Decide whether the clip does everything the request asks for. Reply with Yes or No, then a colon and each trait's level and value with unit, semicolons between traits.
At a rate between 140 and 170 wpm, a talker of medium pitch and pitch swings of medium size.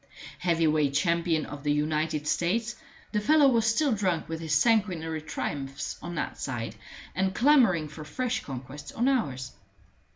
No: average, 155 wpm; medium, 165 Hz; wide, 6.7 semitones